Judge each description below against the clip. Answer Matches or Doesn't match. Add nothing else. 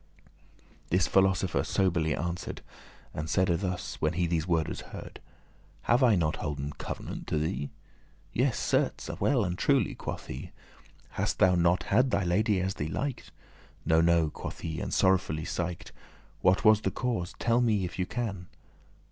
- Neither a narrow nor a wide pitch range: Matches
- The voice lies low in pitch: Matches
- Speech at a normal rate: Matches